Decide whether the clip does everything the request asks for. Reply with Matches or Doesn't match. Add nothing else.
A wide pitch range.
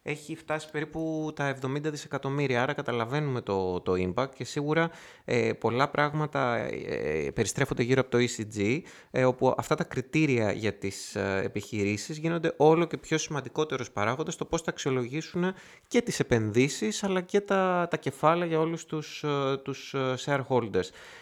Doesn't match